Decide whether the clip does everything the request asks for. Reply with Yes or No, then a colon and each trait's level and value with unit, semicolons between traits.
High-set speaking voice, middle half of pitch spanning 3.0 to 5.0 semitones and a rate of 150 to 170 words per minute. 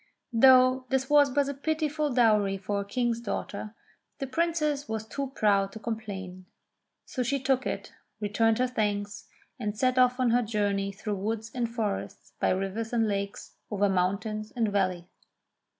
Yes: high, 225 Hz; average, 4.0 semitones; average, 165 wpm